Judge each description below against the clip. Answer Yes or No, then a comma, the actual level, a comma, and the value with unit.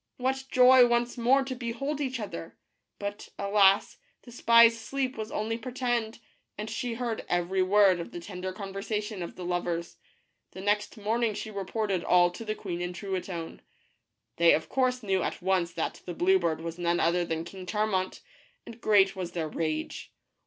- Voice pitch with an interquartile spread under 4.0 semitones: No, average, 4.6 semitones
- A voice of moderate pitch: No, high, 200 Hz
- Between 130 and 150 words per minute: No, average, 175 wpm